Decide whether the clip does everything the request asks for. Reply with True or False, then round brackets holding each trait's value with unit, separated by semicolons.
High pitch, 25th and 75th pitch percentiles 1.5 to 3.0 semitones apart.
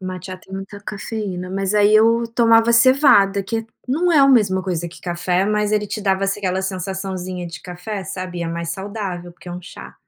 True (195 Hz; 2.7 semitones)